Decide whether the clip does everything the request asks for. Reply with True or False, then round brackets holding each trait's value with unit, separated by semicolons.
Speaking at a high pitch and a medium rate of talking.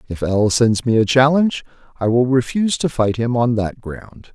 False (125 Hz; 195 wpm)